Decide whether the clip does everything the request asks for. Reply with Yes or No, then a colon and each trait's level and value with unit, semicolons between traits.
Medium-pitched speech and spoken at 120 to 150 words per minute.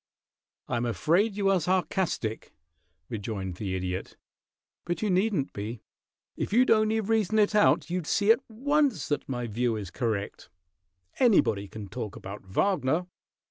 Yes: medium, 160 Hz; average, 145 wpm